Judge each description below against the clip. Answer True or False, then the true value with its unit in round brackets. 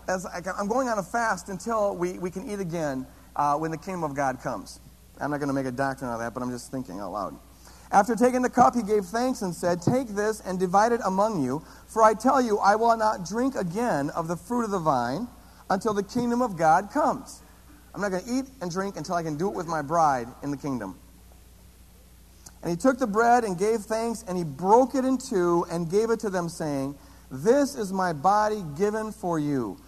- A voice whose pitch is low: False (190 Hz)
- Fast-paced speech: True (235 wpm)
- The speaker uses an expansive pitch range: True (5.9 semitones)